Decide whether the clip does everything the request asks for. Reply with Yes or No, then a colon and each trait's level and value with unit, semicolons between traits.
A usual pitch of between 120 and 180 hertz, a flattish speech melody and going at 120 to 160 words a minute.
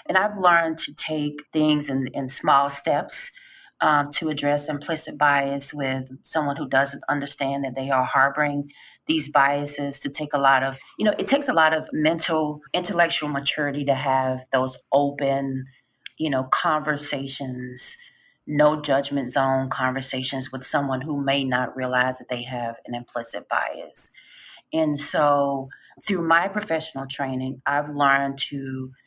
Yes: medium, 140 Hz; narrow, 2.3 semitones; average, 150 wpm